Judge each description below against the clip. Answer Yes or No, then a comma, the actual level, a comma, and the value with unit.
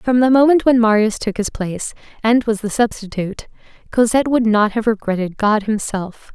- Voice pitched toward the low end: No, high, 220 Hz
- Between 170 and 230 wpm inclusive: Yes, average, 180 wpm